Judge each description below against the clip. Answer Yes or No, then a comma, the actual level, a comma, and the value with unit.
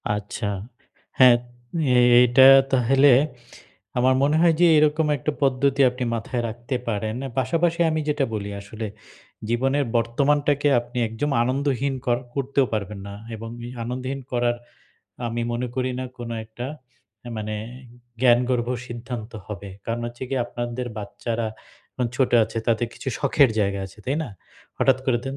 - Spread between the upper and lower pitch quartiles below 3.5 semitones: Yes, average, 2.9 semitones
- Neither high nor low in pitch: No, low, 125 Hz